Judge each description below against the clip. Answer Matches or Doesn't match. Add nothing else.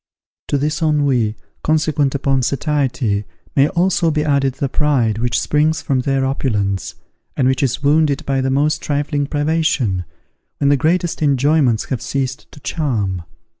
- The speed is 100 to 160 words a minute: Matches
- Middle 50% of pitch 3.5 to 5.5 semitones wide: Doesn't match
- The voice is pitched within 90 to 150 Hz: Matches